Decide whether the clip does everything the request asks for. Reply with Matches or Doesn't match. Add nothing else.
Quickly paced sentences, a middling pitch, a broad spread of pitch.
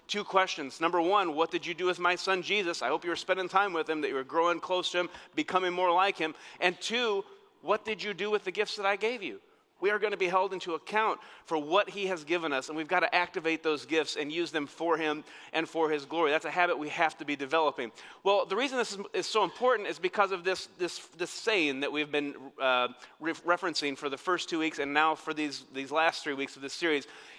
Doesn't match